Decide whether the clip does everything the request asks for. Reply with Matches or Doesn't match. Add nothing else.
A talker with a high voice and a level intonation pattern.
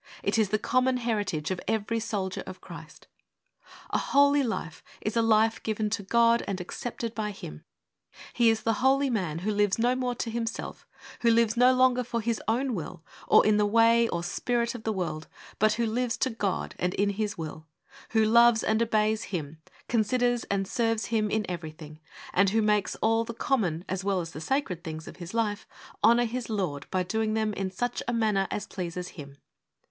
Doesn't match